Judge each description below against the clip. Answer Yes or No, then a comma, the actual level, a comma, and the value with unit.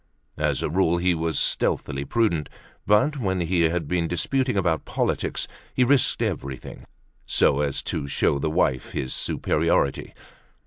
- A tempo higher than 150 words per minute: No, average, 145 wpm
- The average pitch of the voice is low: Yes, very low, 85 Hz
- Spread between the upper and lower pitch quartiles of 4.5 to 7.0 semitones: Yes, average, 4.9 semitones